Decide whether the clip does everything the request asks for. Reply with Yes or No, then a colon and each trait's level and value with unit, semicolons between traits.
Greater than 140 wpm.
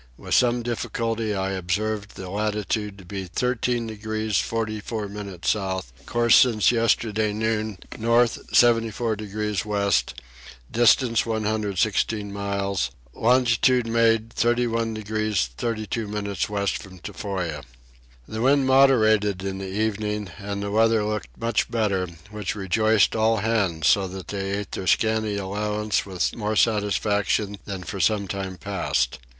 No: slow, 135 wpm